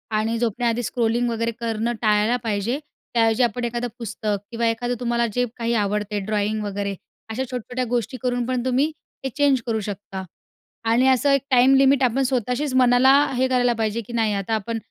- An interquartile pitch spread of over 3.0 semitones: No, narrow, 2.4 semitones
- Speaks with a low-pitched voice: No, high, 235 Hz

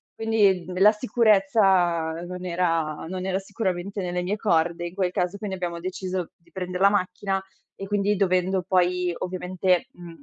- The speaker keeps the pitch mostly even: Yes, narrow, 1.8 semitones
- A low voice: No, medium, 185 Hz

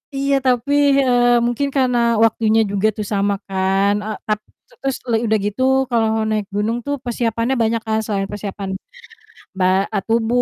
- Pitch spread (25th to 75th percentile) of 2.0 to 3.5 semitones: Yes, average, 2.8 semitones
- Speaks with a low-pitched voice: No, high, 225 Hz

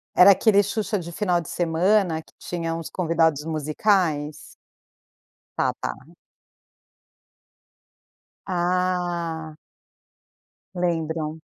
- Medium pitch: Yes, medium, 170 Hz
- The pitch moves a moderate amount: No, narrow, 2.2 semitones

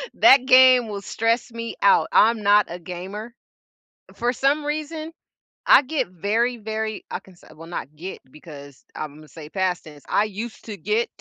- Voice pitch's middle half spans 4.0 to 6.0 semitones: Yes, wide, 5.4 semitones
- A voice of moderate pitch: No, high, 215 Hz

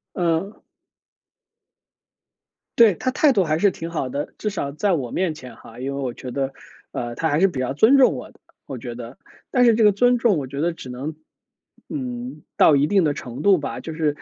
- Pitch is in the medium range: Yes, medium, 160 Hz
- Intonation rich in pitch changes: Yes, wide, 7.0 semitones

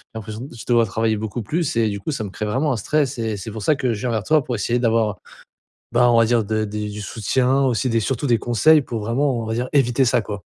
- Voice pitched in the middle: No, low, 115 Hz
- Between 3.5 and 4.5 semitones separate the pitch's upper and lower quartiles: No, average, 2.9 semitones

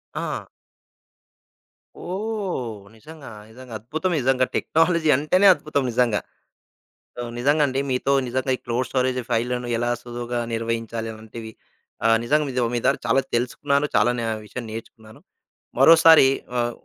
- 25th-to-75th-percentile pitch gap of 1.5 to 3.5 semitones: No, average, 4.0 semitones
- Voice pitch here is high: No, low, 125 Hz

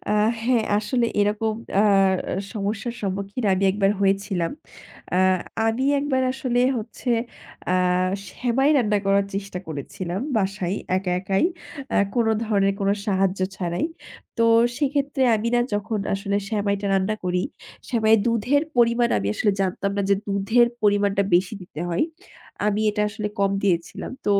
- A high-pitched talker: Yes, high, 205 Hz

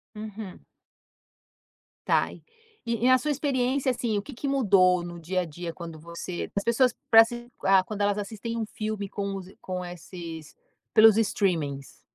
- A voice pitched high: Yes, high, 200 Hz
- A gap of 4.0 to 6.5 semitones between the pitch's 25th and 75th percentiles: Yes, average, 4.6 semitones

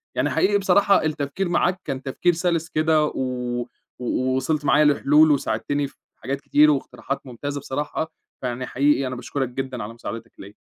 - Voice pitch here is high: No, medium, 140 Hz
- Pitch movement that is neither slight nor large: Yes, average, 3.4 semitones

